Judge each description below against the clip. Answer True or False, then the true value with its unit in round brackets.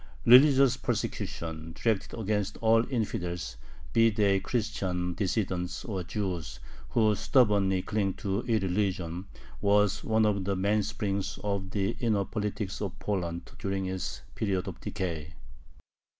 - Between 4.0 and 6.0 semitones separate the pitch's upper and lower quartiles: False (2.7 semitones)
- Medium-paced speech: False (120 wpm)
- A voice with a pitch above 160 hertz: False (100 Hz)